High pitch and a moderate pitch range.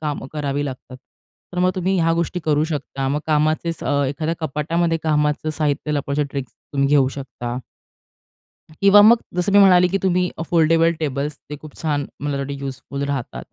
No: medium, 150 Hz; average, 3.1 semitones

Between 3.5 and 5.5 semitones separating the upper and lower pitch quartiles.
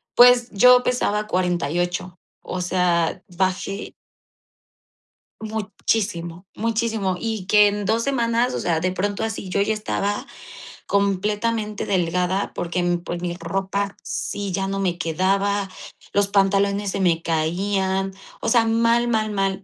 No: average, 2.8 semitones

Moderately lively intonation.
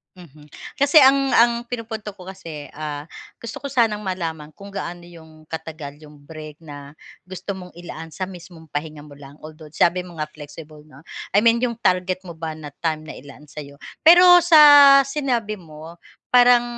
No: wide, 6.2 semitones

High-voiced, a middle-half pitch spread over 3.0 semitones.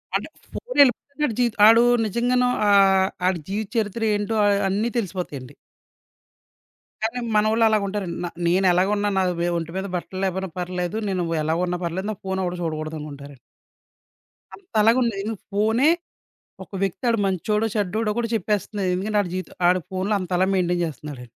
Yes: high, 195 Hz; average, 3.4 semitones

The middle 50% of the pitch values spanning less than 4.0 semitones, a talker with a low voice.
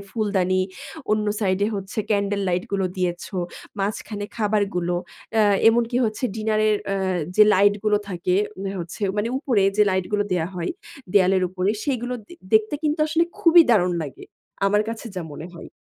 No: average, 2.8 semitones; high, 205 Hz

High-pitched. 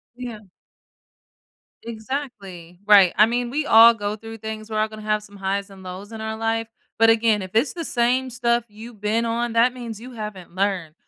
Yes: high, 220 Hz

